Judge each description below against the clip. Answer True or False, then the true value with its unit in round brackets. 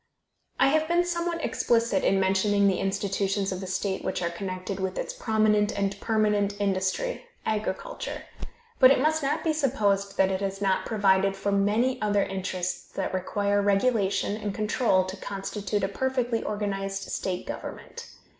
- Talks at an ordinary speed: True (165 wpm)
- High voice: True (200 Hz)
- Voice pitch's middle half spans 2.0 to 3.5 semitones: True (2.5 semitones)